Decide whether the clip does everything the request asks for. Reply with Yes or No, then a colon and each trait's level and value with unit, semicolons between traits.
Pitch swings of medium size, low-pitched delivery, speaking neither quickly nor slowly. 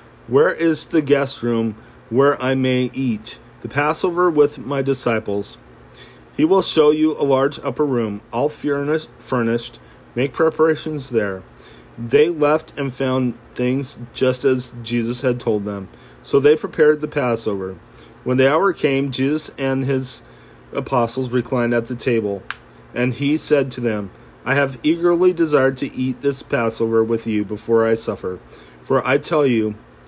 Yes: average, 3.4 semitones; low, 130 Hz; average, 155 wpm